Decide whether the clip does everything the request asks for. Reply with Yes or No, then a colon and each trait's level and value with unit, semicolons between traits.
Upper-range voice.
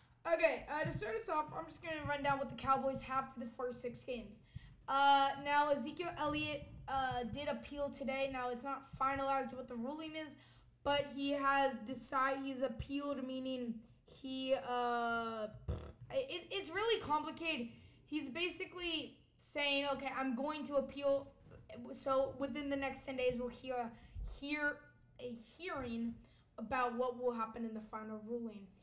Yes: very high, 270 Hz